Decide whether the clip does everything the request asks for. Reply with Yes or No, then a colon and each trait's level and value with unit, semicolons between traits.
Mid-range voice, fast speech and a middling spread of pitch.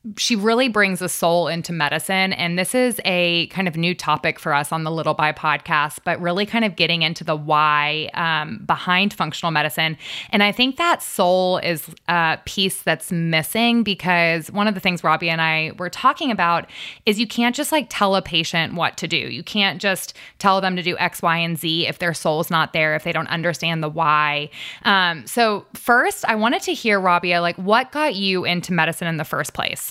Yes: medium, 175 Hz; fast, 215 wpm; average, 3.8 semitones